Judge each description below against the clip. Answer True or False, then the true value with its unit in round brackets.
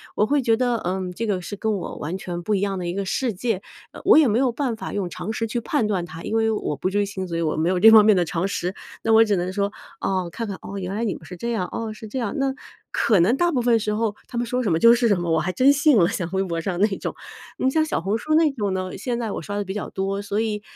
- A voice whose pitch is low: False (205 Hz)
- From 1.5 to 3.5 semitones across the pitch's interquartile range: False (3.9 semitones)